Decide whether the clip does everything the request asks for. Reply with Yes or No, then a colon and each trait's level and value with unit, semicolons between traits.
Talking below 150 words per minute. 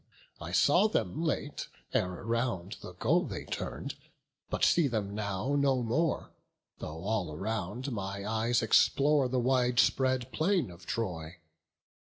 Yes: average, 140 wpm